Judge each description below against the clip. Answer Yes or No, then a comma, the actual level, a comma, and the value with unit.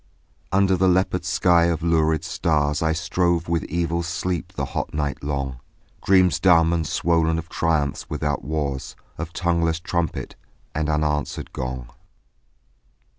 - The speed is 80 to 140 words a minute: Yes, slow, 135 wpm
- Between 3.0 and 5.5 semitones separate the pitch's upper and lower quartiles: No, narrow, 2.4 semitones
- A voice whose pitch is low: Yes, very low, 80 Hz